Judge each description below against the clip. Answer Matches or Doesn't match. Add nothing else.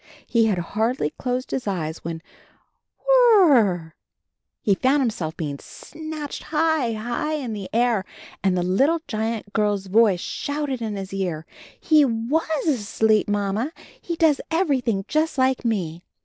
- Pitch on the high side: Matches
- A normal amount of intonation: Doesn't match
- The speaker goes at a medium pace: Matches